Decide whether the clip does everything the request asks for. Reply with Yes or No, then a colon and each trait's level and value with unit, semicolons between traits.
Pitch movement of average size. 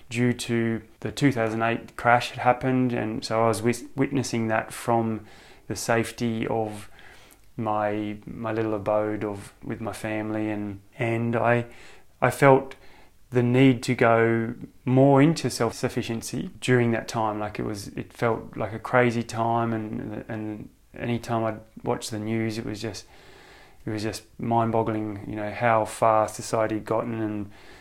No: narrow, 1.9 semitones